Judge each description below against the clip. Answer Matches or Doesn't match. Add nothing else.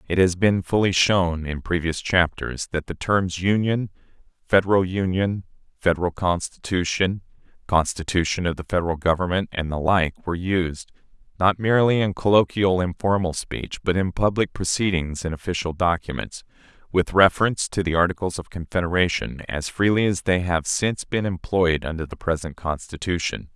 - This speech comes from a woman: Doesn't match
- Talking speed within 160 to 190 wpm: Doesn't match